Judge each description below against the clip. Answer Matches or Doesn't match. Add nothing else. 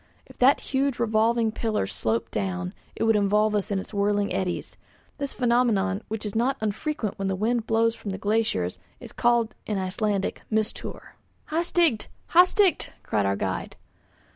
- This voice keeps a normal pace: Matches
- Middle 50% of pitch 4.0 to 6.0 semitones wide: Doesn't match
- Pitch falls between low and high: Doesn't match